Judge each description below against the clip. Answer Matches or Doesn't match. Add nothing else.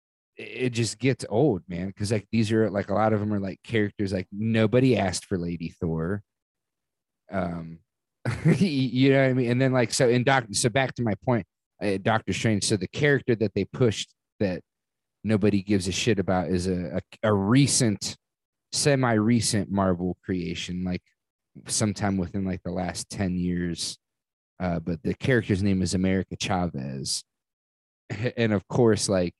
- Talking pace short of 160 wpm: Doesn't match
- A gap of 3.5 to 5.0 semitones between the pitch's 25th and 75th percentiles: Matches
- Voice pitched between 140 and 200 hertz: Doesn't match